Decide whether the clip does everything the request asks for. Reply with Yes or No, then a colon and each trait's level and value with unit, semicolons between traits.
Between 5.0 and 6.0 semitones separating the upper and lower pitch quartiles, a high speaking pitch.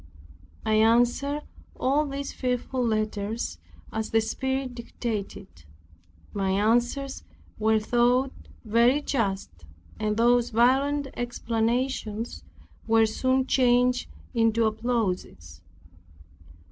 No: average, 2.8 semitones; high, 235 Hz